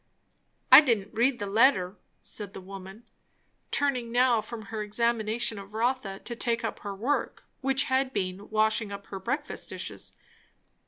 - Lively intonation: No, average, 3.7 semitones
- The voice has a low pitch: No, high, 225 Hz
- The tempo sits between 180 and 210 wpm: No, average, 155 wpm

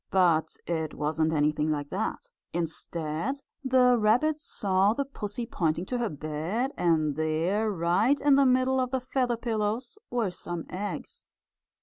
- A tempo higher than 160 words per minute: No, average, 145 wpm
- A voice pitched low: No, high, 200 Hz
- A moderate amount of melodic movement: No, wide, 7.6 semitones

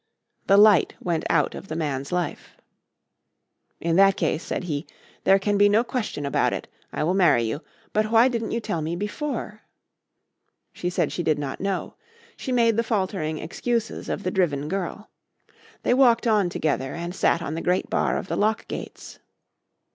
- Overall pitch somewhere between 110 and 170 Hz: No, medium, 185 Hz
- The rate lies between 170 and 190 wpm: Yes, average, 180 wpm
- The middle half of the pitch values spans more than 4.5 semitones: Yes, average, 5.2 semitones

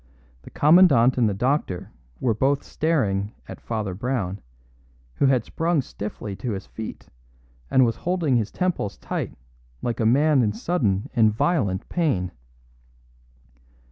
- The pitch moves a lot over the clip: Yes, wide, 5.9 semitones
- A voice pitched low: Yes, low, 120 Hz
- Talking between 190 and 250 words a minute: No, average, 140 wpm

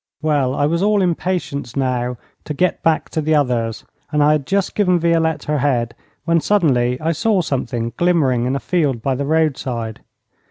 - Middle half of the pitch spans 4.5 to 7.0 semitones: Yes, average, 4.8 semitones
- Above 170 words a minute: Yes, average, 185 wpm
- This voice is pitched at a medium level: Yes, medium, 150 Hz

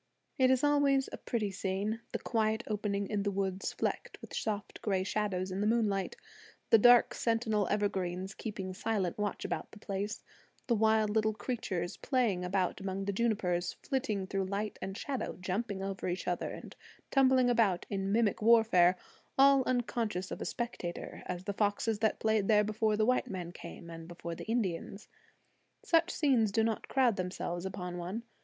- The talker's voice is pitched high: Yes, high, 210 Hz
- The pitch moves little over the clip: No, average, 3.1 semitones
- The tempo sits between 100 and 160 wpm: No, average, 175 wpm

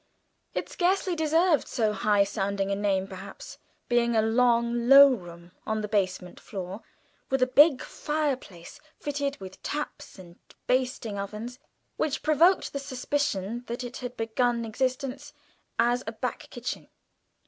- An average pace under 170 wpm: Yes, average, 140 wpm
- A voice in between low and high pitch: No, high, 240 Hz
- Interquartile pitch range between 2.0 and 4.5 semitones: No, average, 5.3 semitones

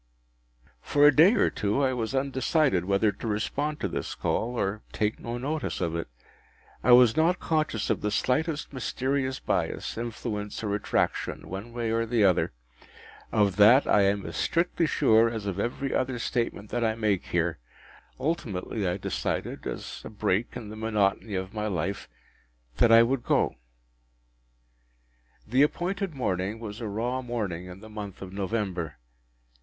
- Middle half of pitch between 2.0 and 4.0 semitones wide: No, average, 4.5 semitones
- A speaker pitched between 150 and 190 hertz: No, low, 110 Hz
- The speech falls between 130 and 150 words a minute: No, average, 160 wpm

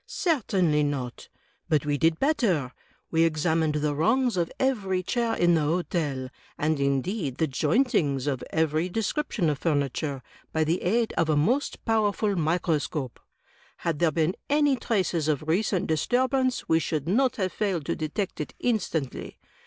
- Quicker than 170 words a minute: No, average, 160 wpm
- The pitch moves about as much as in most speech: No, wide, 5.9 semitones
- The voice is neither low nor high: Yes, medium, 165 Hz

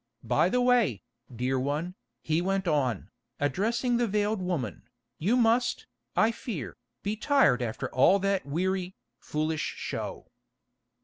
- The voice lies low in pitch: No, medium, 185 Hz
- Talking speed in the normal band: No, slow, 130 wpm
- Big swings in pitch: Yes, wide, 7.3 semitones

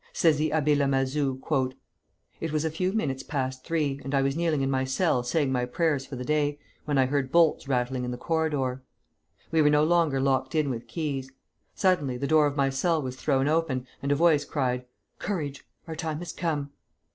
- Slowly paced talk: No, fast, 205 wpm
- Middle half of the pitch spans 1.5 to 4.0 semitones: Yes, average, 3.1 semitones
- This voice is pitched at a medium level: Yes, medium, 145 Hz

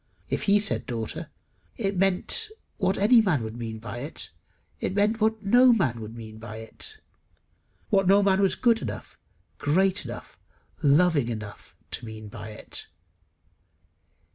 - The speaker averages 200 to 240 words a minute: No, average, 150 wpm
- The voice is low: No, medium, 180 Hz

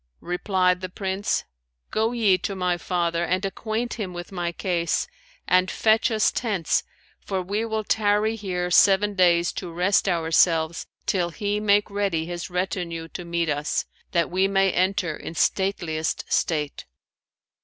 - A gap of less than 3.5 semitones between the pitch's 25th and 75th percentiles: Yes, average, 2.9 semitones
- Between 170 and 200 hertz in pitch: Yes, medium, 185 Hz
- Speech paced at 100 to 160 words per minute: Yes, average, 150 wpm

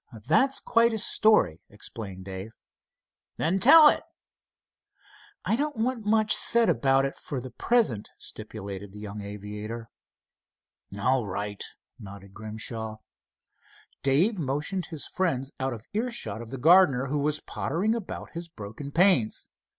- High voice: No, low, 135 Hz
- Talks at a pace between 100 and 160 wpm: Yes, slow, 135 wpm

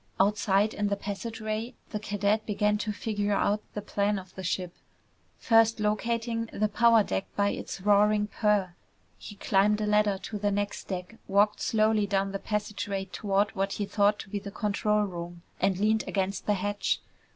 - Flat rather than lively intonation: Yes, narrow, 1.3 semitones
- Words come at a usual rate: Yes, average, 175 wpm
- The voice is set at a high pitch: Yes, high, 205 Hz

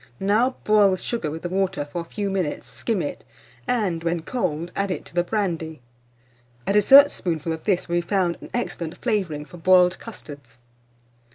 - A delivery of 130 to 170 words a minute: No, average, 180 wpm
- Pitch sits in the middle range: Yes, medium, 180 Hz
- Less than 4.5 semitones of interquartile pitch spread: Yes, average, 3.8 semitones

